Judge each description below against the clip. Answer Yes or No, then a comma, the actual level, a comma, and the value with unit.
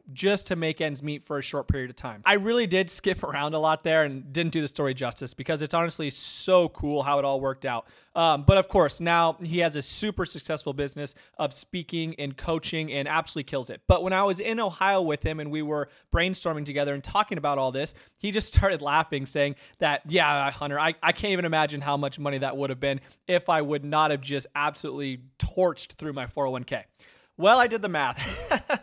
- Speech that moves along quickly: Yes, fast, 225 wpm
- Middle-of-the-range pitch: Yes, medium, 155 Hz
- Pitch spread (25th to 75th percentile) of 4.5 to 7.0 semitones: No, average, 3.6 semitones